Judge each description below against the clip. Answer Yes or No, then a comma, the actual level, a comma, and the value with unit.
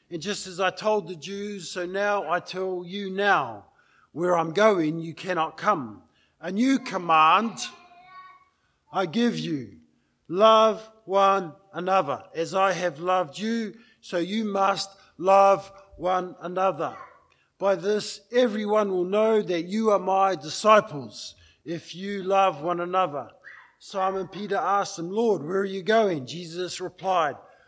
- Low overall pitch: No, high, 190 Hz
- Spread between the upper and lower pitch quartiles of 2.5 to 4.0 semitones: Yes, average, 2.9 semitones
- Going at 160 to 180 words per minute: No, average, 140 wpm